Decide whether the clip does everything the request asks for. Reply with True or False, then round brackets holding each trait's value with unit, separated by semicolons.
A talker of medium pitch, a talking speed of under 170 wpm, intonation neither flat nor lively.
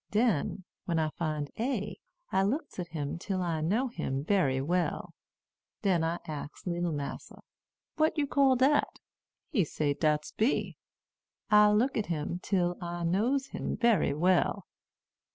False (180 Hz; 150 wpm; 6.0 semitones)